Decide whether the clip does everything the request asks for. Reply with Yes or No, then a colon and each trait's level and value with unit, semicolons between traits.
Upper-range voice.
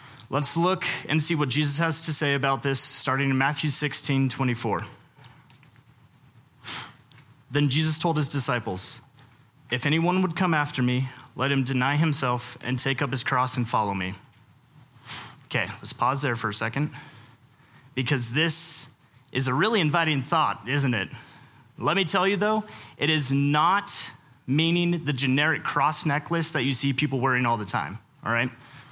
No: low, 135 Hz